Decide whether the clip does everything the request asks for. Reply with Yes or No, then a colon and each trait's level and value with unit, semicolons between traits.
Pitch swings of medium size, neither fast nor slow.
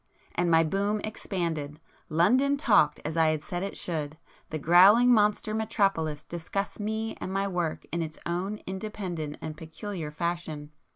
Yes: average, 4.6 semitones; average, 150 wpm